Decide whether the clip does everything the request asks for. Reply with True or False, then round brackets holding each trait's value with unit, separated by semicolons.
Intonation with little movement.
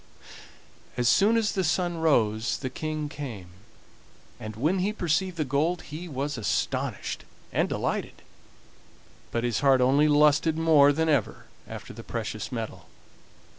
False (3.8 semitones)